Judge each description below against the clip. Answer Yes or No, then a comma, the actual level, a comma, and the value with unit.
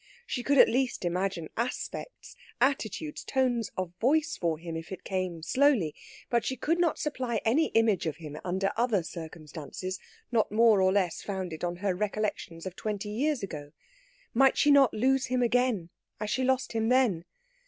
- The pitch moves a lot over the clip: Yes, wide, 6.2 semitones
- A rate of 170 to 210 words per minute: Yes, average, 175 wpm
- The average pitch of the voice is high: Yes, high, 215 Hz